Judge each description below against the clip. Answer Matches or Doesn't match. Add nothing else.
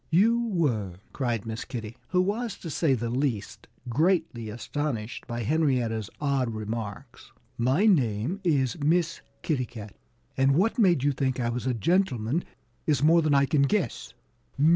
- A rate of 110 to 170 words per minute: Matches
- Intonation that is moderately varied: Doesn't match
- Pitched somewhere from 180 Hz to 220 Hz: Doesn't match